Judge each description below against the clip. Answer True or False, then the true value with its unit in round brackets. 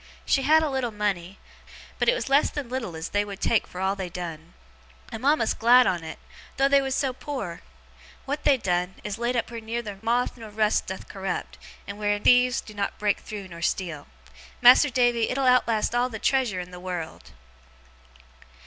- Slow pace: False (195 wpm)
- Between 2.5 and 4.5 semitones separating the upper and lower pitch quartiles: False (4.9 semitones)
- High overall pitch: True (220 Hz)